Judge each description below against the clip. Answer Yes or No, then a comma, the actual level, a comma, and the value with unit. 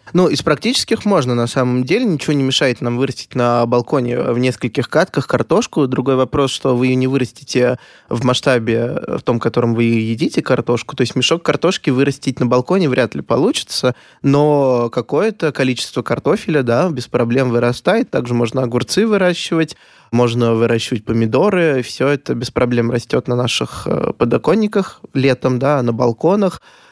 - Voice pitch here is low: Yes, low, 130 Hz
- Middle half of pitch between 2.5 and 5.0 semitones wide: Yes, average, 3.6 semitones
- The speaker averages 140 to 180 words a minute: Yes, fast, 160 wpm